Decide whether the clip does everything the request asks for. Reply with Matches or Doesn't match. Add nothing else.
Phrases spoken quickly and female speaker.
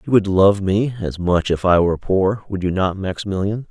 Doesn't match